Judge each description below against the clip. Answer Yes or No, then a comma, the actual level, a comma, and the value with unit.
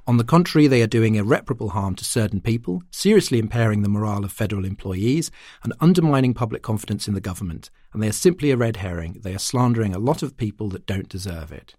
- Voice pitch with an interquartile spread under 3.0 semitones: No, average, 4.7 semitones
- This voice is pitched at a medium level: No, low, 110 Hz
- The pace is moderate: No, fast, 220 wpm